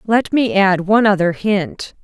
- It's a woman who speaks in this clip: Yes, female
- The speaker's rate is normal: Yes, average, 175 wpm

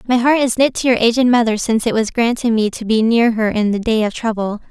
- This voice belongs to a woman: Yes, female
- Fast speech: Yes, fast, 280 wpm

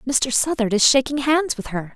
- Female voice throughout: Yes, female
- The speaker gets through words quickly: Yes, fast, 215 wpm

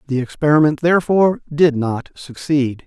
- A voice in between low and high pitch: Yes, medium, 145 Hz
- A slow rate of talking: Yes, slow, 125 wpm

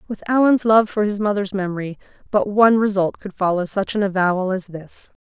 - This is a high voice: Yes, high, 200 Hz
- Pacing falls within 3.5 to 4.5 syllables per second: No, 5.6 syllables/s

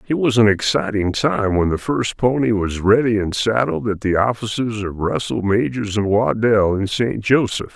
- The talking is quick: No, average, 185 wpm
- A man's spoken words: Yes, male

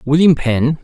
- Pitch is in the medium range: Yes, medium, 145 Hz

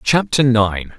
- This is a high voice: No, low, 120 Hz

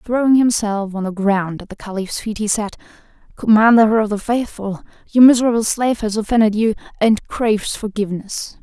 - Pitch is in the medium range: No, high, 215 Hz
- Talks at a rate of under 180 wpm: Yes, average, 165 wpm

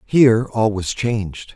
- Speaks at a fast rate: No, average, 155 wpm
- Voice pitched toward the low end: Yes, low, 110 Hz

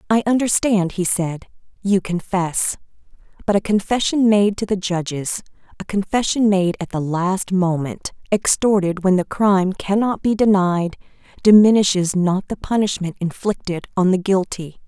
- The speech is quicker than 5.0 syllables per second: No, 4.6 syllables/s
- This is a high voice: Yes, high, 195 Hz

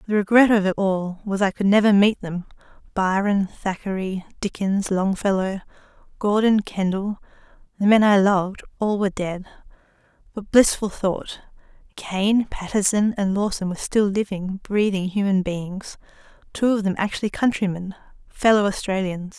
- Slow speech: Yes, slow, 130 wpm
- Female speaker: Yes, female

